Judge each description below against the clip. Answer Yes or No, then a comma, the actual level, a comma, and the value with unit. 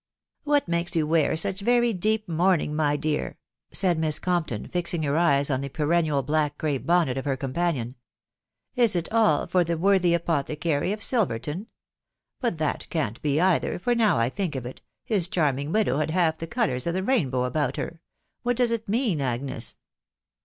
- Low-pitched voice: No, medium, 165 Hz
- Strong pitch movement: No, average, 4.7 semitones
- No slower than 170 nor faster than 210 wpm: Yes, average, 185 wpm